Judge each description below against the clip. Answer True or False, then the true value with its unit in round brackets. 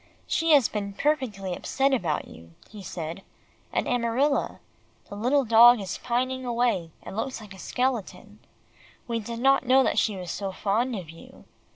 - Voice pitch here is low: False (230 Hz)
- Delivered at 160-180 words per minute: True (170 wpm)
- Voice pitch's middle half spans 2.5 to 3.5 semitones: False (4.8 semitones)